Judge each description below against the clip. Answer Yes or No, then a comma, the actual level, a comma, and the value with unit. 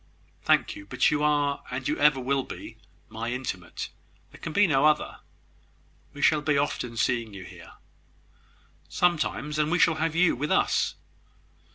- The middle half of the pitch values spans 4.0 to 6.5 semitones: No, average, 3.4 semitones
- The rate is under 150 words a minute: No, average, 160 wpm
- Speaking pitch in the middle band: Yes, medium, 145 Hz